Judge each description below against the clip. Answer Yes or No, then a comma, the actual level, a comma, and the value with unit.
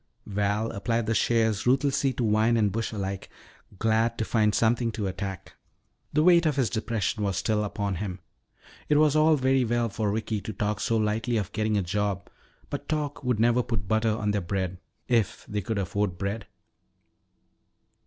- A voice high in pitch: No, low, 110 Hz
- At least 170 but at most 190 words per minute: Yes, average, 180 wpm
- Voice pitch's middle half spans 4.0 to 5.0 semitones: No, narrow, 2.5 semitones